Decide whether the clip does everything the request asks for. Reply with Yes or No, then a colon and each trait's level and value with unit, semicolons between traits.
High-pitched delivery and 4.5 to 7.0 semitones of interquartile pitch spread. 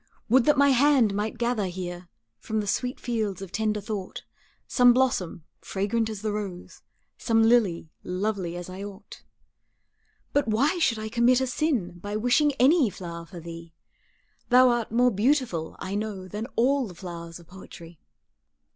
Yes: high, 215 Hz; average, 5.0 semitones